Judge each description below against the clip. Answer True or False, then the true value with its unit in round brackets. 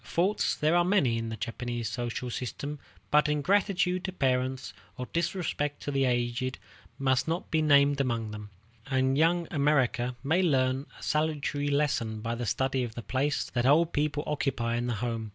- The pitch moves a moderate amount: True (3.8 semitones)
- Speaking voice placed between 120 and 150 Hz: True (135 Hz)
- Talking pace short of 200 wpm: True (175 wpm)